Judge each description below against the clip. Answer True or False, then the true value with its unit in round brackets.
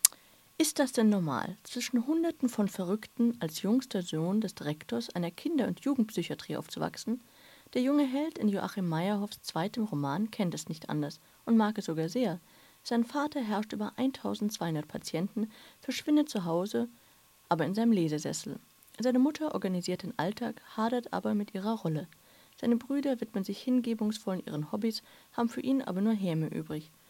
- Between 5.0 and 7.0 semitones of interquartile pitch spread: True (5.4 semitones)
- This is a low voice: False (215 Hz)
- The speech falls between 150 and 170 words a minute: True (160 wpm)